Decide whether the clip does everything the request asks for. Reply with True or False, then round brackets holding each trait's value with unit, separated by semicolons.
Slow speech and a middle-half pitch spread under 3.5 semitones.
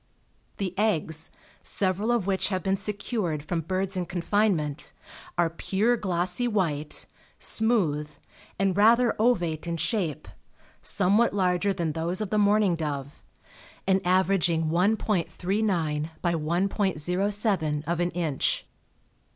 False (120 wpm; 3.8 semitones)